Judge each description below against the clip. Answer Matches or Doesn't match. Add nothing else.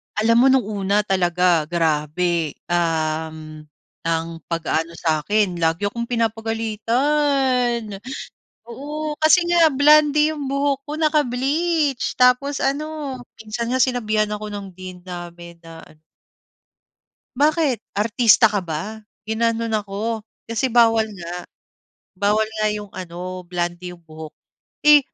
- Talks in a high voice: Matches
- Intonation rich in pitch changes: Matches